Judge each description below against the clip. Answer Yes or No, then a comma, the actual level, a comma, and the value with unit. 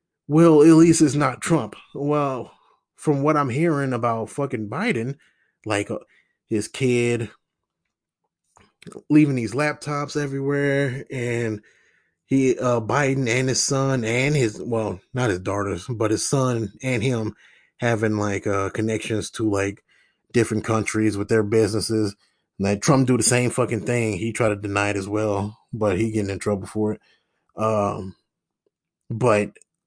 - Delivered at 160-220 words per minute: No, average, 150 wpm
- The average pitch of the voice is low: Yes, low, 115 Hz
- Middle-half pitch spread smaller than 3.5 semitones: No, average, 4.0 semitones